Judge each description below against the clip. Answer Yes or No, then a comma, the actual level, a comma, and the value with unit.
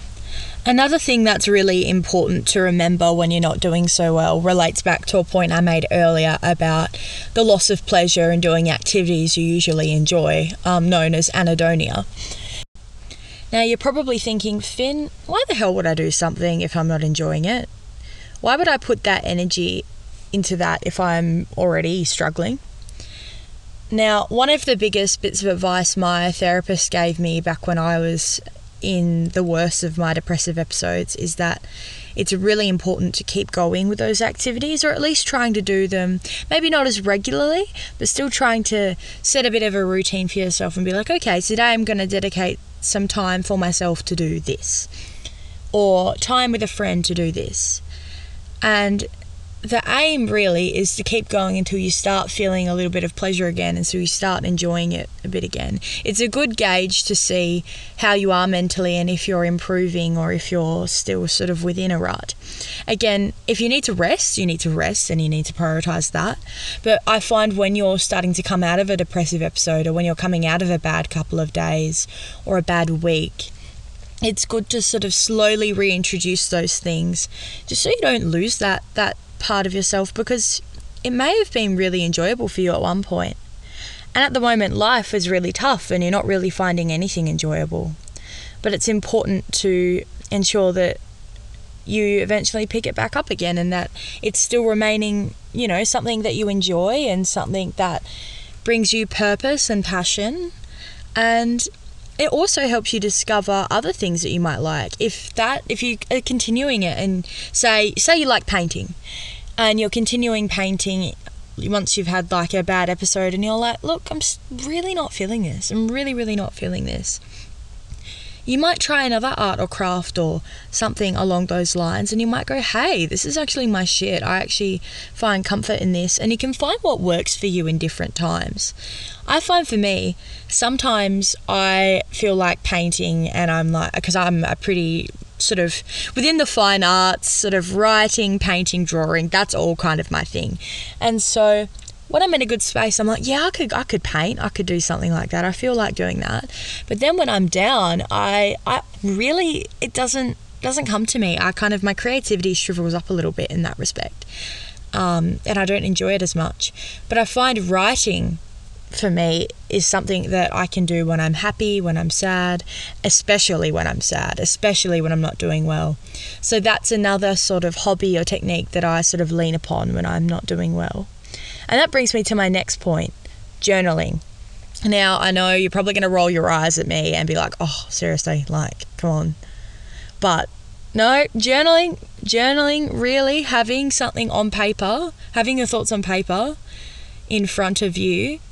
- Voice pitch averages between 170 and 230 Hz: Yes, medium, 185 Hz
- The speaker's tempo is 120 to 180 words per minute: No, average, 190 wpm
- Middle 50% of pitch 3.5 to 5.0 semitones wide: Yes, average, 4.3 semitones